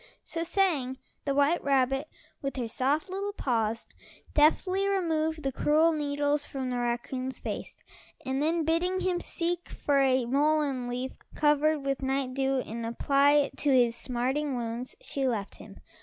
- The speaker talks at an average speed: Yes, average, 155 wpm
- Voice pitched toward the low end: No, very high, 280 Hz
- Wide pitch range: No, average, 3.4 semitones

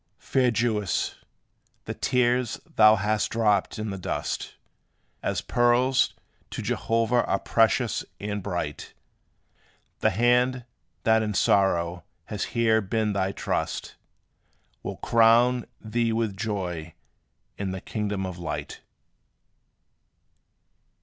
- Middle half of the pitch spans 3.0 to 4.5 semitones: Yes, average, 3.3 semitones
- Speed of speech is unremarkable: No, slow, 110 wpm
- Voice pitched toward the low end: Yes, low, 110 Hz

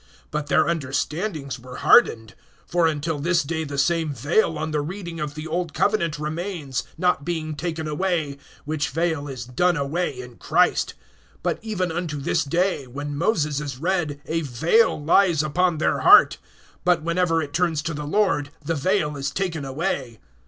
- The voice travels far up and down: No, average, 3.2 semitones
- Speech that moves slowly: No, average, 170 wpm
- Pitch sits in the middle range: Yes, medium, 155 Hz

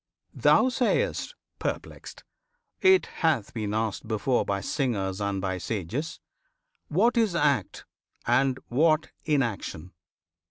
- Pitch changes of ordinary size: No, wide, 8.0 semitones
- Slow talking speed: Yes, slow, 110 wpm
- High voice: No, low, 125 Hz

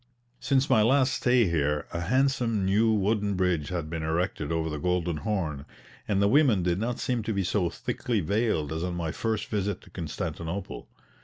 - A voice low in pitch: Yes, very low, 95 Hz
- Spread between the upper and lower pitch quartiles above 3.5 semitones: Yes, average, 5.1 semitones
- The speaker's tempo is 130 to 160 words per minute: No, average, 185 wpm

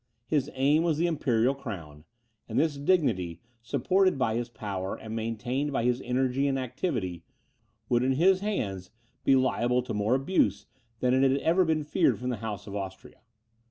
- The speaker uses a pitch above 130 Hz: No, low, 125 Hz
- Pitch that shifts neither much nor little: Yes, average, 4.6 semitones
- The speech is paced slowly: No, average, 170 wpm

